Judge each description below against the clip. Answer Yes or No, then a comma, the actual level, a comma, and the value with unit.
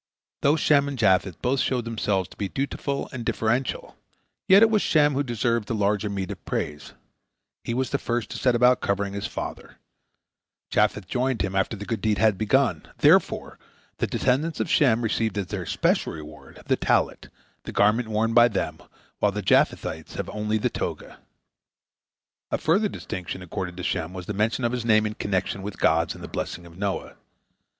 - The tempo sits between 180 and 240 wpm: Yes, average, 190 wpm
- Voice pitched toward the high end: No, low, 110 Hz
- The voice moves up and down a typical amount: Yes, average, 4.4 semitones